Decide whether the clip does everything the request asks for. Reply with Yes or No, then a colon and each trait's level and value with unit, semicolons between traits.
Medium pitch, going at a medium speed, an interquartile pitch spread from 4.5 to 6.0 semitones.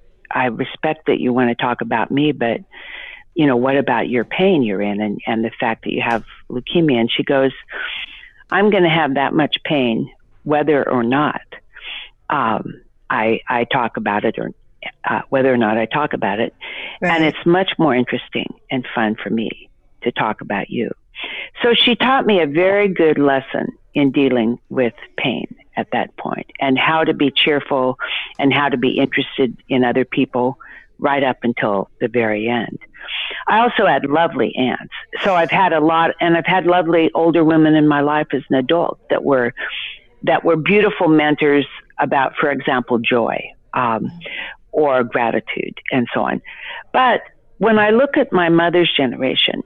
Yes: medium, 145 Hz; average, 180 wpm; average, 5.2 semitones